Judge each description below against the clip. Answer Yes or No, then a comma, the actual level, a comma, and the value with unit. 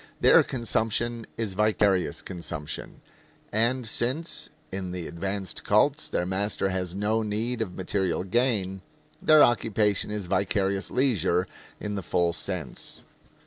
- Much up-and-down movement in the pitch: No, average, 3.4 semitones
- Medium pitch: No, low, 100 Hz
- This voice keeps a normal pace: No, slow, 125 wpm